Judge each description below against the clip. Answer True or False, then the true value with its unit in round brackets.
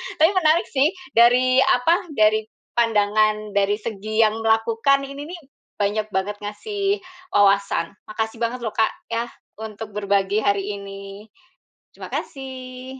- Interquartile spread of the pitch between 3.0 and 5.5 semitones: True (3.8 semitones)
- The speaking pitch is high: True (220 Hz)